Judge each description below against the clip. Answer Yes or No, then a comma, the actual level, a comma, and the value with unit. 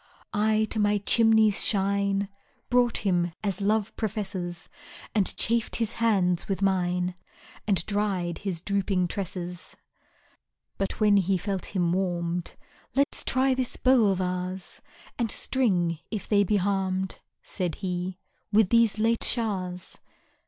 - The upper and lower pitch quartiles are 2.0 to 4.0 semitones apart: Yes, average, 3.1 semitones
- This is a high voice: Yes, high, 195 Hz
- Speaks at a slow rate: Yes, slow, 130 wpm